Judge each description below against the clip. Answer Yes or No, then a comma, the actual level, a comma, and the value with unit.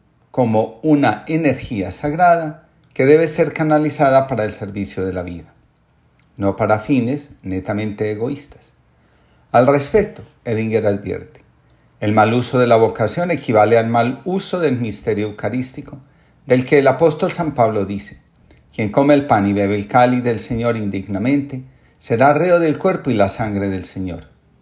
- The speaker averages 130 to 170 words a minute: Yes, average, 155 wpm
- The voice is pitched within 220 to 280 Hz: No, low, 120 Hz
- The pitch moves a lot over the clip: Yes, wide, 5.7 semitones